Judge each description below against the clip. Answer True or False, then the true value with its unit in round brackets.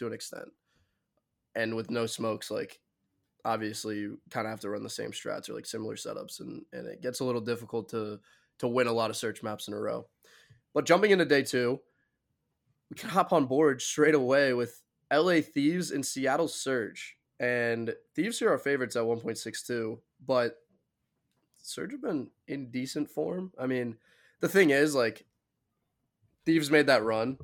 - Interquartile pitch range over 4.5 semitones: False (3.8 semitones)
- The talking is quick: False (180 wpm)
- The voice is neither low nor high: False (125 Hz)